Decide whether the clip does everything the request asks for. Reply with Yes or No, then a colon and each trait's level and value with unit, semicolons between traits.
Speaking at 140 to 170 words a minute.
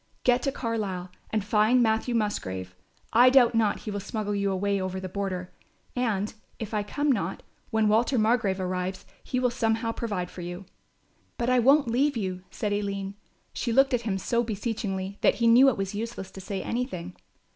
No: average, 190 wpm